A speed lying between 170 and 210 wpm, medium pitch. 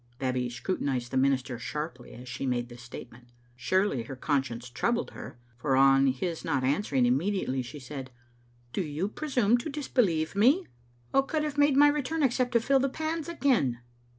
Yes: average, 175 wpm; medium, 150 Hz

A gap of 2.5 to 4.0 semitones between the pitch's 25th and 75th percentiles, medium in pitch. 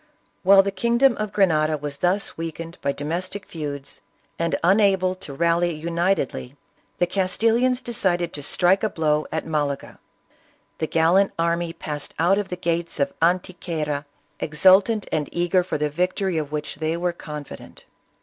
Yes: average, 3.7 semitones; medium, 170 Hz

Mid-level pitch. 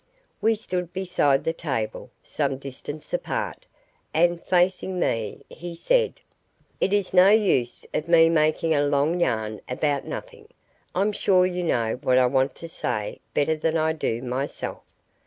Yes: medium, 160 Hz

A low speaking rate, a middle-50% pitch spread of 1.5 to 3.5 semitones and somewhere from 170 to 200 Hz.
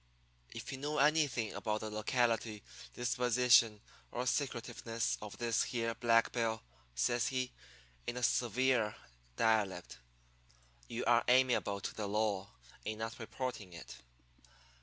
No: slow, 125 wpm; narrow, 2.5 semitones; low, 115 Hz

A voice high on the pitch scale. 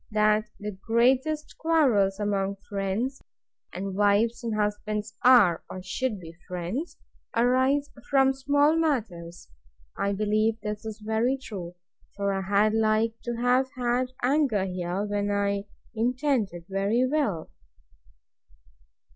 Yes: high, 215 Hz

